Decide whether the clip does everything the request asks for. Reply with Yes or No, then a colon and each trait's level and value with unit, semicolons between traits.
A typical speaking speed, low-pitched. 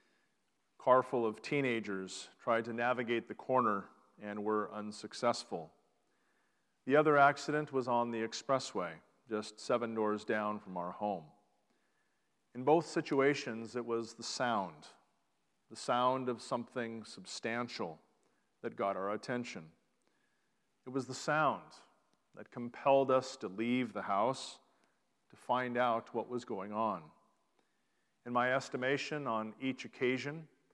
No: slow, 130 wpm; low, 120 Hz